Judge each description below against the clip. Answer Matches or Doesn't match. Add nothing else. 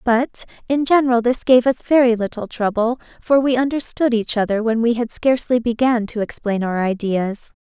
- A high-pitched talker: Matches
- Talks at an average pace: Matches